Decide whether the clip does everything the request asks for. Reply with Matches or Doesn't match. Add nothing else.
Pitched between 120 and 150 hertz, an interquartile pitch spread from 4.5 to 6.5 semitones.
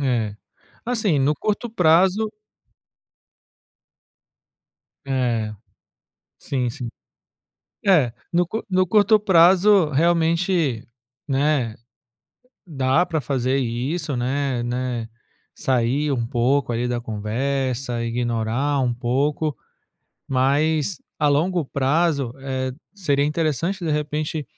Matches